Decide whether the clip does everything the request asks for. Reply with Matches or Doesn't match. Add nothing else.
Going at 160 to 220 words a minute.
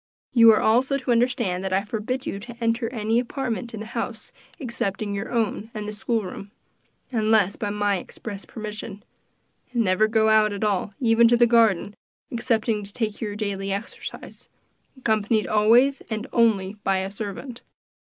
Matches